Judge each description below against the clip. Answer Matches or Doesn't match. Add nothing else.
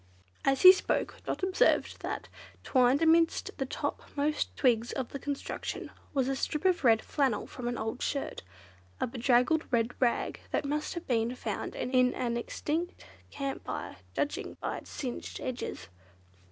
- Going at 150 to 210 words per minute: Matches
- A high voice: Matches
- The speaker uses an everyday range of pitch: Matches